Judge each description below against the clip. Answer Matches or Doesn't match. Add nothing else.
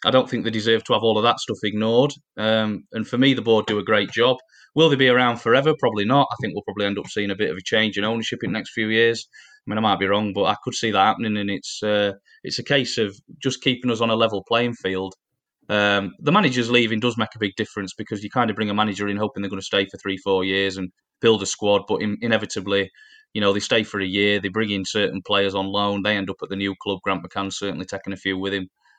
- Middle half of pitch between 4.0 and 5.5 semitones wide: Doesn't match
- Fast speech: Matches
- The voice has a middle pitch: Doesn't match